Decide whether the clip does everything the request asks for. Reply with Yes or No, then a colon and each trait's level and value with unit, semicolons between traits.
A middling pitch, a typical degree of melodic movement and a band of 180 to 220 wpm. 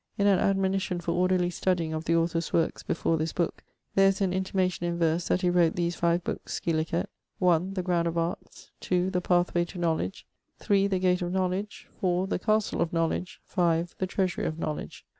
No: medium, 175 Hz; narrow, 1.9 semitones; average, 200 wpm